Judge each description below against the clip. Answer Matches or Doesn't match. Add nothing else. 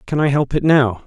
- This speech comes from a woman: Doesn't match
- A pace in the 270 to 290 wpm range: Matches